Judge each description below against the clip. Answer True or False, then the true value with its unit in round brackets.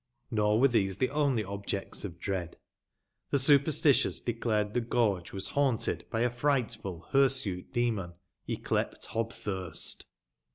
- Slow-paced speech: True (125 wpm)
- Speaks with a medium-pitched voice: False (115 Hz)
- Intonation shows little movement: False (4.7 semitones)